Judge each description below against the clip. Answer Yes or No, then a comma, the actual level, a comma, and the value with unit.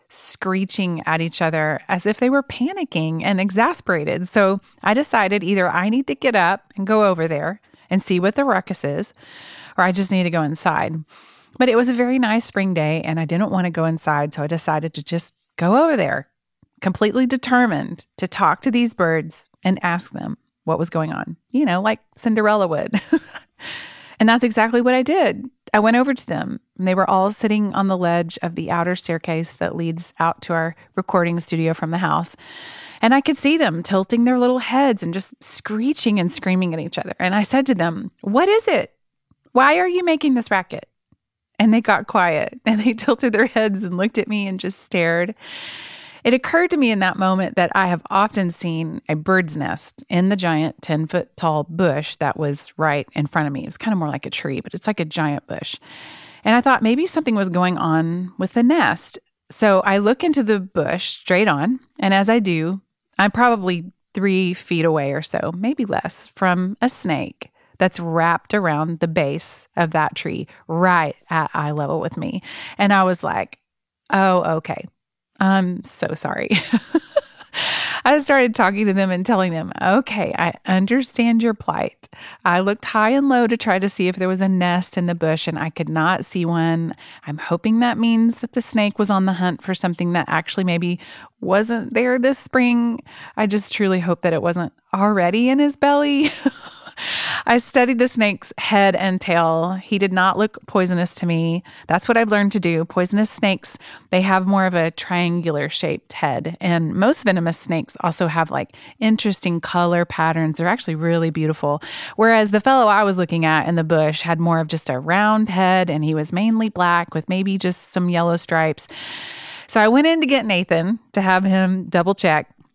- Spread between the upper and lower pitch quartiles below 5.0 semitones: No, average, 5.3 semitones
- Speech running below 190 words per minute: No, average, 200 wpm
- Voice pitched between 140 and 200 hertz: Yes, high, 190 Hz